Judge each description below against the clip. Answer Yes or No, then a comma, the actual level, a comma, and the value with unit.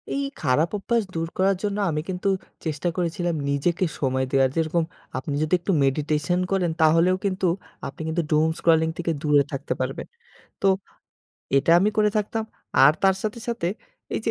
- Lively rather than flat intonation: No, average, 3.9 semitones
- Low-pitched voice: No, medium, 165 Hz